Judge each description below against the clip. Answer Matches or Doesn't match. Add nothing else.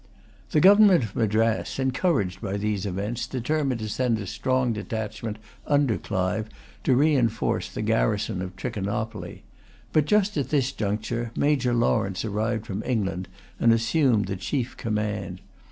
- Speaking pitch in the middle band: Doesn't match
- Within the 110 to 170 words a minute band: Matches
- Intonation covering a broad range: Doesn't match